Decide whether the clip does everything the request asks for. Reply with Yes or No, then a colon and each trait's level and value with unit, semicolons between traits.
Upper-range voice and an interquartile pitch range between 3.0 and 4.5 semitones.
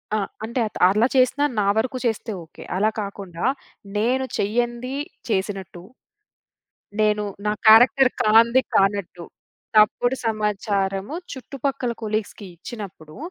Yes: high, 215 Hz; average, 3.5 semitones